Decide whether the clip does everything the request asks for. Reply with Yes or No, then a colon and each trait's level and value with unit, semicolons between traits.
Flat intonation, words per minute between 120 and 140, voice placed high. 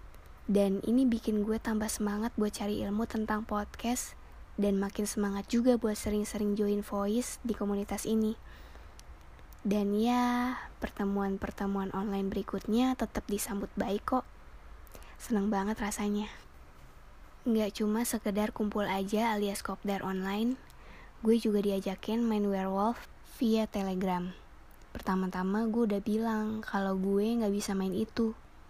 Yes: narrow, 2.0 semitones; average, 125 wpm; high, 205 Hz